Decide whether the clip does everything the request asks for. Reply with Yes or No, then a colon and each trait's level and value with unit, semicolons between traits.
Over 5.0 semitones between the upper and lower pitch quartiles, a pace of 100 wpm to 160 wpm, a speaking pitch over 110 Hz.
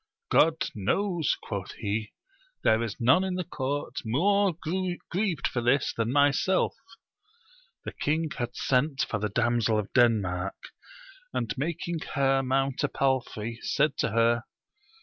Yes: wide, 5.6 semitones; slow, 135 wpm; low, 135 Hz